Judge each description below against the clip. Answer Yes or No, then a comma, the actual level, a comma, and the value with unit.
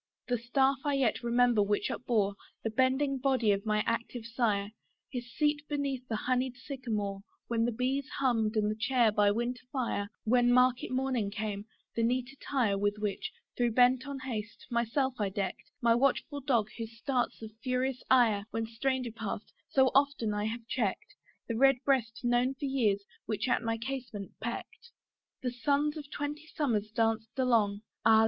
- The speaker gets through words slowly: No, average, 170 wpm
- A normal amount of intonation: Yes, average, 3.3 semitones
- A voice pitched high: Yes, high, 240 Hz